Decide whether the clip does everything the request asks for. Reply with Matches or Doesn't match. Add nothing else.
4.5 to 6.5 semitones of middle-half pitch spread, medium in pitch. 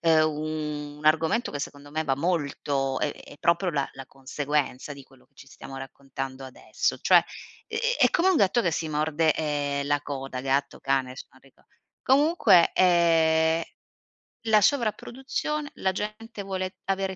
Matches